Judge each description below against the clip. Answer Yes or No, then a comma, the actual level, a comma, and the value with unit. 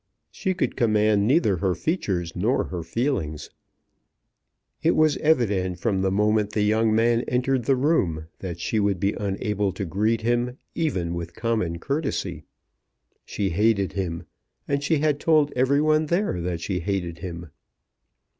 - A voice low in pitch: Yes, low, 105 Hz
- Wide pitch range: Yes, wide, 6.2 semitones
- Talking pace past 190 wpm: No, average, 155 wpm